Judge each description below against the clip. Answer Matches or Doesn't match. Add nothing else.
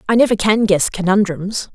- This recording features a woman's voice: Matches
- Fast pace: Doesn't match